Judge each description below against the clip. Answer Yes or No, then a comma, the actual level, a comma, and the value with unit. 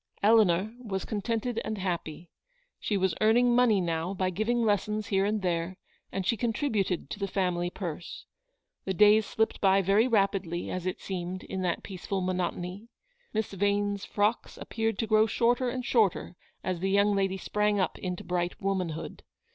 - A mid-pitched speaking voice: No, high, 195 Hz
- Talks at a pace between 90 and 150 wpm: No, average, 165 wpm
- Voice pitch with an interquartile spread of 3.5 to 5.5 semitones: No, average, 2.9 semitones